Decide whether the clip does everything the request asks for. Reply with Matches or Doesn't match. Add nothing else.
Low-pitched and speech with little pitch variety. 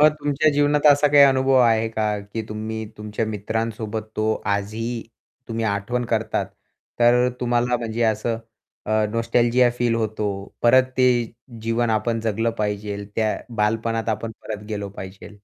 Matches